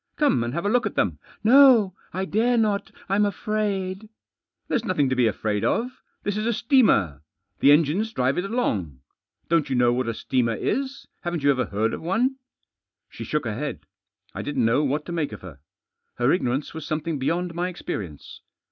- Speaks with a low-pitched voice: No, medium, 165 Hz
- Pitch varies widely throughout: Yes, wide, 9.0 semitones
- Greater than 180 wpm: Yes, average, 195 wpm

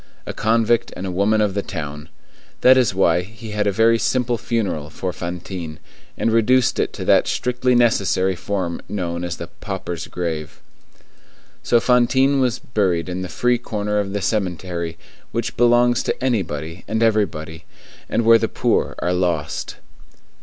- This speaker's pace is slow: No, average, 160 wpm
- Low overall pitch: Yes, low, 100 Hz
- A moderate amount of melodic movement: Yes, average, 4.8 semitones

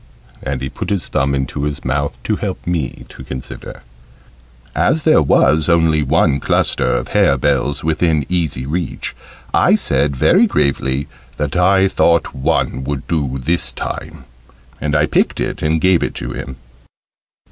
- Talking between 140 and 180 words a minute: Yes, average, 160 wpm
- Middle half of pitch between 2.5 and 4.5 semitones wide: Yes, average, 3.8 semitones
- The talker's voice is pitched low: Yes, very low, 75 Hz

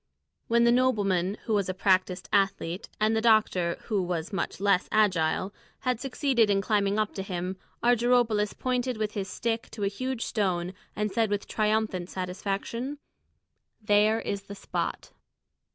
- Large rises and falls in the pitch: No, average, 3.0 semitones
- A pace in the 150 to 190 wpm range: Yes, average, 155 wpm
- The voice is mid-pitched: No, high, 205 Hz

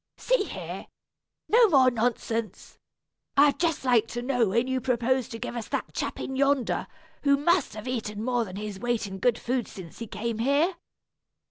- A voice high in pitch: Yes, high, 245 Hz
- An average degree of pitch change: Yes, average, 3.4 semitones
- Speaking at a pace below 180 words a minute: No, average, 185 wpm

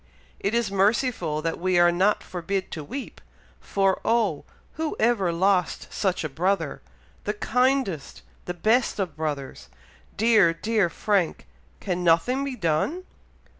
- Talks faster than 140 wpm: No, slow, 135 wpm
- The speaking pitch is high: Yes, high, 195 Hz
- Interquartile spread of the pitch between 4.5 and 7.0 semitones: Yes, average, 5.0 semitones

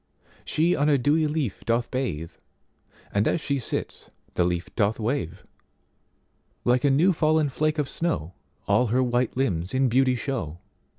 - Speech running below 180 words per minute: Yes, average, 140 wpm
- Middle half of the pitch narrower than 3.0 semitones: No, wide, 5.4 semitones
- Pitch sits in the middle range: No, low, 130 Hz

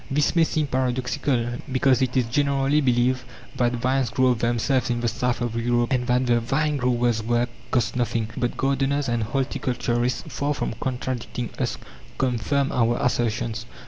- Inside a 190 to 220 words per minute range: No, average, 165 wpm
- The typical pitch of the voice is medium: No, low, 125 Hz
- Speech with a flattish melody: Yes, narrow, 2.1 semitones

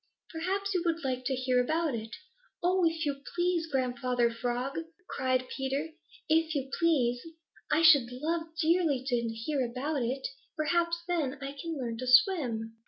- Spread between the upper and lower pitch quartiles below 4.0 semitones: No, average, 4.8 semitones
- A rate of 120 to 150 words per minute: No, average, 160 wpm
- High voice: Yes, very high, 275 Hz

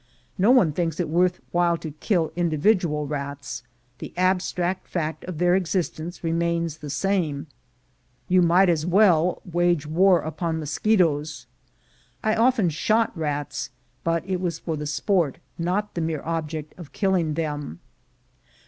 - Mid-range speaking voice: Yes, medium, 170 Hz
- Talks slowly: No, average, 150 wpm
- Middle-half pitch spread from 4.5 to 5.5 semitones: No, average, 3.1 semitones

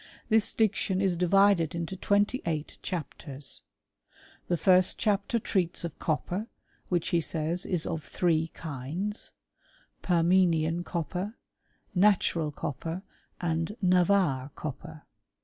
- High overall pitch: No, medium, 175 Hz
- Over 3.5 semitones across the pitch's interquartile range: No, average, 3.1 semitones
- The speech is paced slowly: Yes, slow, 110 wpm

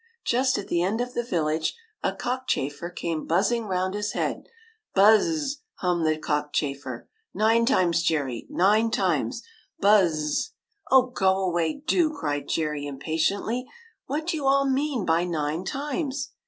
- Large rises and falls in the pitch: Yes, wide, 8.2 semitones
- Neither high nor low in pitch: No, high, 195 Hz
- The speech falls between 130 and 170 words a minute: No, average, 180 wpm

